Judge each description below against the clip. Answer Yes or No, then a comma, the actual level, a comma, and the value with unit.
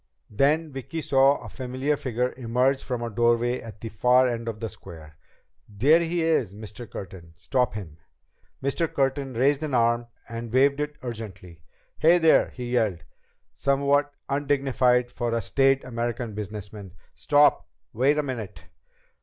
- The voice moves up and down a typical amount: Yes, average, 4.0 semitones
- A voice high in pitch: No, low, 125 Hz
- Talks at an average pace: Yes, average, 150 wpm